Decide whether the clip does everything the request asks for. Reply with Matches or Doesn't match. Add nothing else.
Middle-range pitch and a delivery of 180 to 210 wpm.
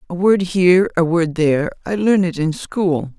Matches